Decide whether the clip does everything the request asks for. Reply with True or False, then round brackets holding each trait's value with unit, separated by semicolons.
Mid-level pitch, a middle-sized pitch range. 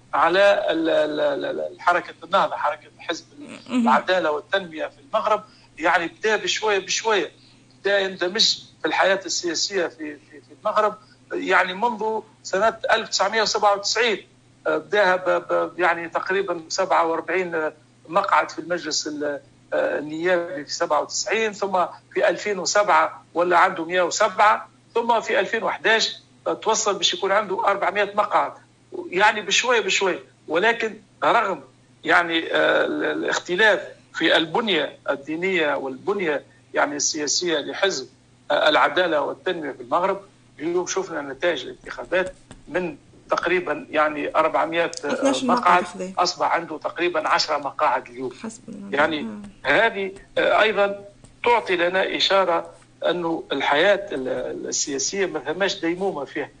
True (180 Hz; 4.6 semitones)